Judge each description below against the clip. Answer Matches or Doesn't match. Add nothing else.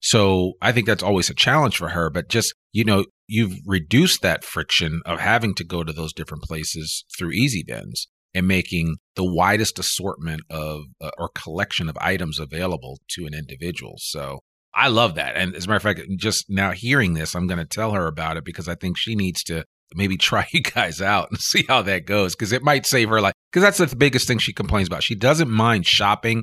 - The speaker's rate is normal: Doesn't match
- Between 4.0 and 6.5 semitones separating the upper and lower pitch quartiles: Matches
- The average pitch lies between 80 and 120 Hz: Matches